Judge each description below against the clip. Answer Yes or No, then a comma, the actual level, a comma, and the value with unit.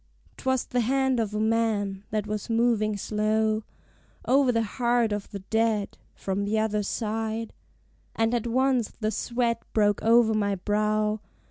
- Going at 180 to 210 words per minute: No, average, 150 wpm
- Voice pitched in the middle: No, high, 220 Hz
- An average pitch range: No, narrow, 1.9 semitones